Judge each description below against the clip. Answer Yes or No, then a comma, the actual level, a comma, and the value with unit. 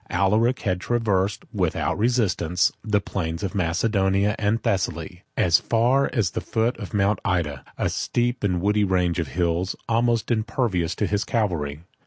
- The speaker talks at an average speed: Yes, average, 155 wpm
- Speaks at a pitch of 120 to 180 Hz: No, low, 100 Hz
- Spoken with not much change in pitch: No, average, 4.1 semitones